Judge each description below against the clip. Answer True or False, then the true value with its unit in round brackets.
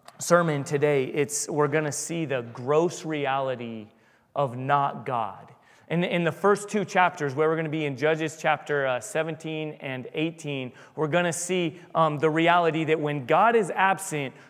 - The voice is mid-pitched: True (155 Hz)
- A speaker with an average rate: True (160 wpm)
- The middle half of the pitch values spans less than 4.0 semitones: True (2.5 semitones)